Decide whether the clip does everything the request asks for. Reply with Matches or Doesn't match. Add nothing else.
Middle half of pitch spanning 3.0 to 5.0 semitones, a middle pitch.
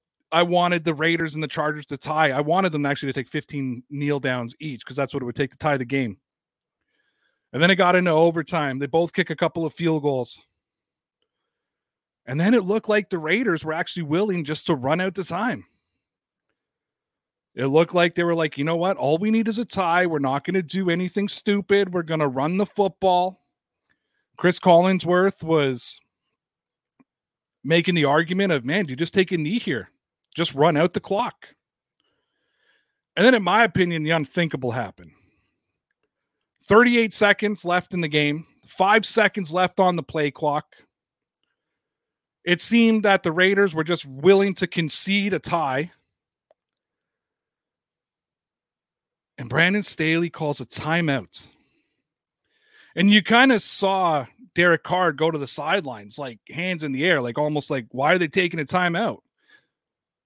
Matches